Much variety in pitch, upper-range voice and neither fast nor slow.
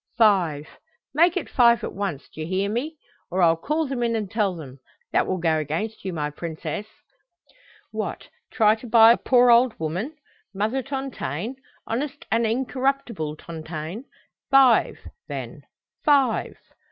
Yes: wide, 7.3 semitones; high, 220 Hz; average, 145 wpm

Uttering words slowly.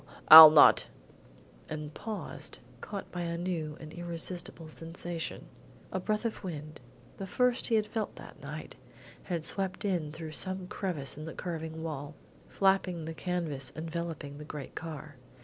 No: average, 155 wpm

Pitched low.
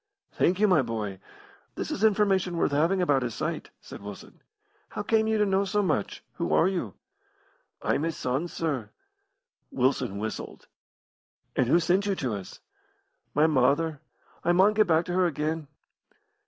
No: medium, 165 Hz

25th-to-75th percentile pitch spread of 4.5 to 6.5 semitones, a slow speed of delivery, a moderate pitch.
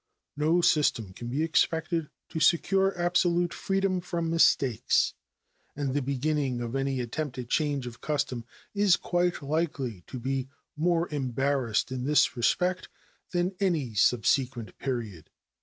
Yes: average, 5.2 semitones; slow, 130 wpm; medium, 145 Hz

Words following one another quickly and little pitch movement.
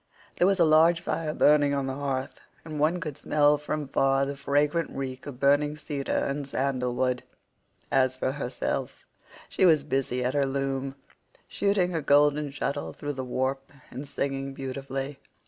No: average, 165 wpm; narrow, 1.7 semitones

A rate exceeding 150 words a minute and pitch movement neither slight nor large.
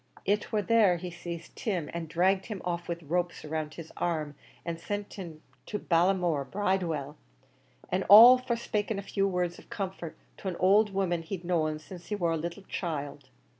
Yes: average, 185 wpm; average, 3.1 semitones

